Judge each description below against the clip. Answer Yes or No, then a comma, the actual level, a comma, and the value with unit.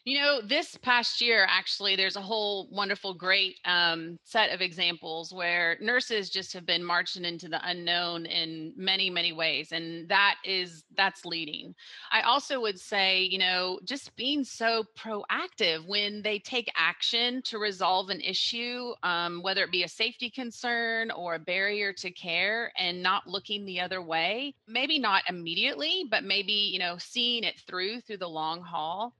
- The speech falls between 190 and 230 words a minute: No, average, 170 wpm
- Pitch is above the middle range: Yes, high, 195 Hz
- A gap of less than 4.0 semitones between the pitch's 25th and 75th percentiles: No, average, 4.5 semitones